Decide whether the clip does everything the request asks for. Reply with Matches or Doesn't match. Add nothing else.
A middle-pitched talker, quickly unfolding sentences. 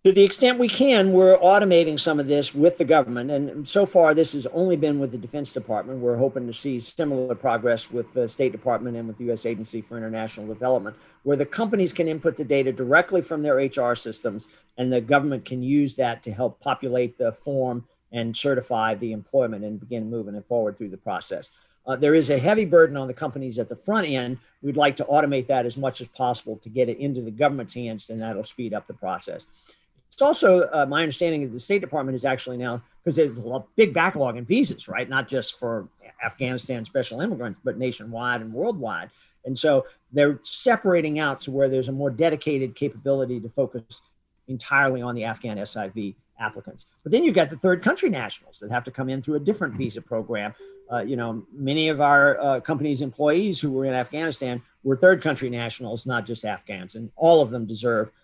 Doesn't match